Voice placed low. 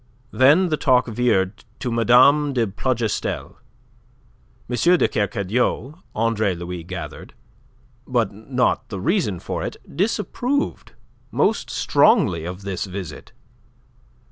Yes: low, 115 Hz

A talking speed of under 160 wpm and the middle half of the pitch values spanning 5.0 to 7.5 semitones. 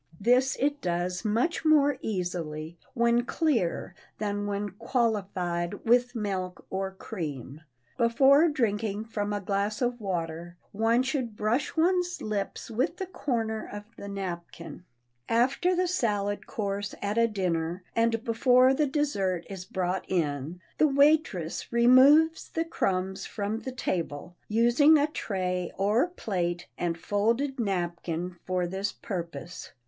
Yes: slow, 135 wpm; wide, 5.6 semitones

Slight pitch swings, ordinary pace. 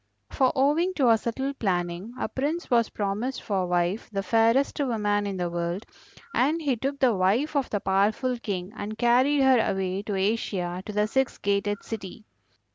No: average, 5.2 semitones; average, 180 wpm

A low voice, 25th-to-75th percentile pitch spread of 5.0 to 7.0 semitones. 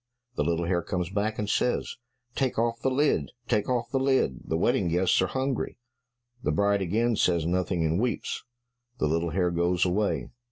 Yes: very low, 95 Hz; wide, 5.6 semitones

